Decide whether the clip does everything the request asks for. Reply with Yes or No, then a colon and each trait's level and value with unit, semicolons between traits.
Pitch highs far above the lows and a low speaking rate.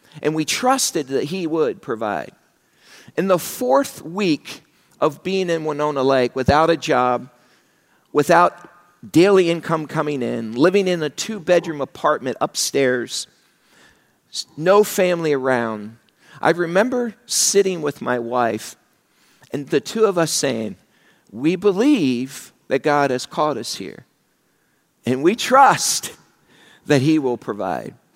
Yes: wide, 6.0 semitones; slow, 130 wpm